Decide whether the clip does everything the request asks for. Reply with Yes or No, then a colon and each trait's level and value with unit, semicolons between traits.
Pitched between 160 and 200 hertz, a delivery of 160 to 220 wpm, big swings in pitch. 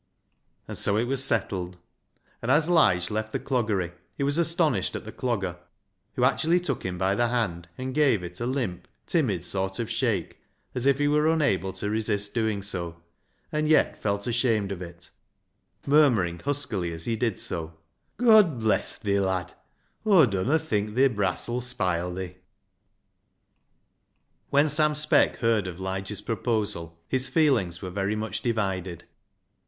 No: low, 110 Hz; average, 165 wpm; wide, 6.2 semitones